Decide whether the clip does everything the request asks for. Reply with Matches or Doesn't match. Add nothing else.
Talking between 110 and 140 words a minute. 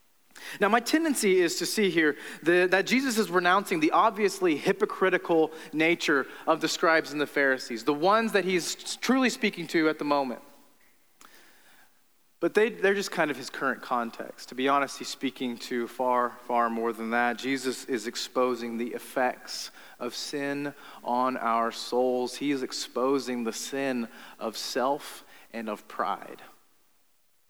Doesn't match